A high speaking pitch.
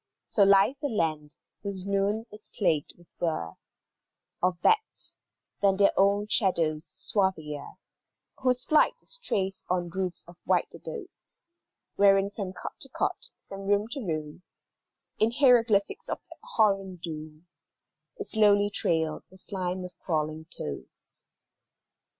Yes: high, 195 Hz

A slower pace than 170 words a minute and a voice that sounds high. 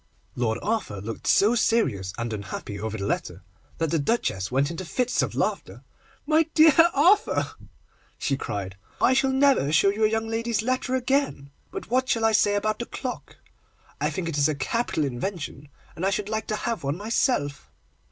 No: average, 185 wpm; high, 200 Hz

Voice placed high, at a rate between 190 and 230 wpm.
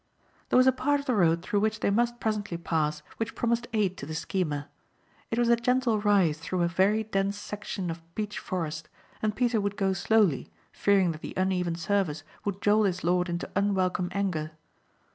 Yes: high, 195 Hz; average, 195 wpm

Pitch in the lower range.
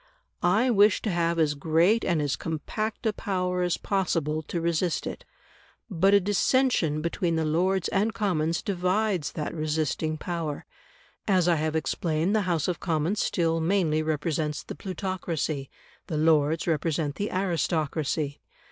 No: medium, 170 Hz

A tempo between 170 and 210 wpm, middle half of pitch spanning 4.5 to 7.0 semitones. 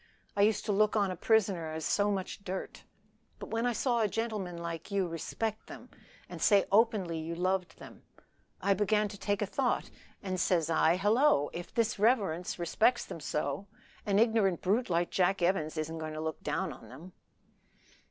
No: average, 180 wpm; average, 4.0 semitones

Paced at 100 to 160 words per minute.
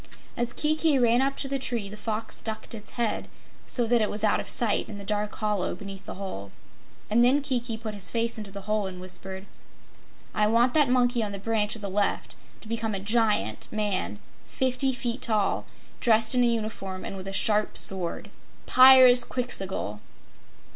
No: average, 190 wpm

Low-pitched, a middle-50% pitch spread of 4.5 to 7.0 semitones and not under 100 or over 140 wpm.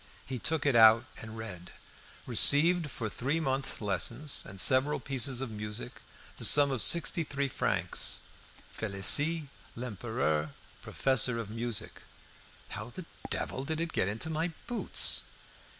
Yes: low, 130 Hz; average, 5.0 semitones; slow, 135 wpm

